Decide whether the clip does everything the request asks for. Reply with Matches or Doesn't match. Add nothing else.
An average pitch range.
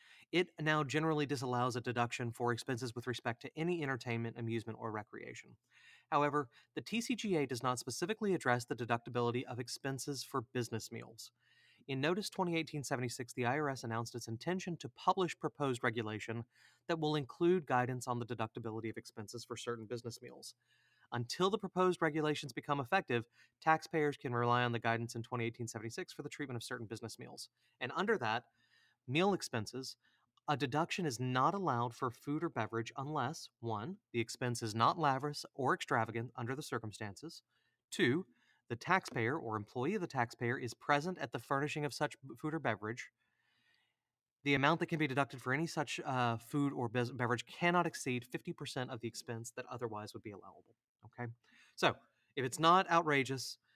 Matches